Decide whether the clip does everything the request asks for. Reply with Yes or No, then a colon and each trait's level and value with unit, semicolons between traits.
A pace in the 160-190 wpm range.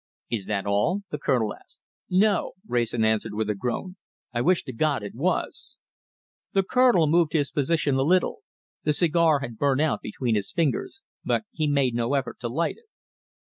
Yes: average, 180 wpm